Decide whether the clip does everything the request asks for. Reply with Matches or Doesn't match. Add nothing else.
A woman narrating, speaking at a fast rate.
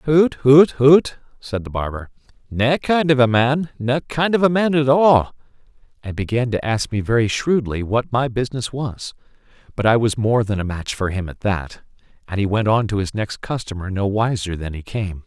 Doesn't match